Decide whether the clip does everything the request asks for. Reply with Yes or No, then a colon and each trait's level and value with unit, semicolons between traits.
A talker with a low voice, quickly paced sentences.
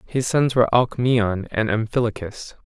No: low, 115 Hz; slow, 135 wpm